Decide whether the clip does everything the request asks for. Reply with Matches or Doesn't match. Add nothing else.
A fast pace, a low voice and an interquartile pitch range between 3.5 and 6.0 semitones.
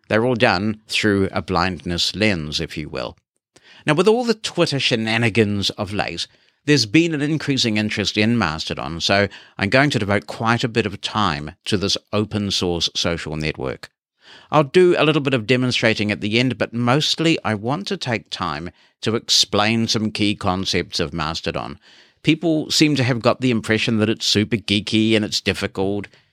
Doesn't match